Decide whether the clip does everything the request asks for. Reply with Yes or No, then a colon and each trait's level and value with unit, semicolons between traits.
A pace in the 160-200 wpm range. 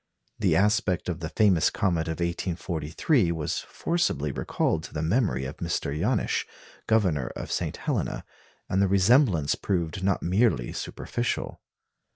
No: average, 140 wpm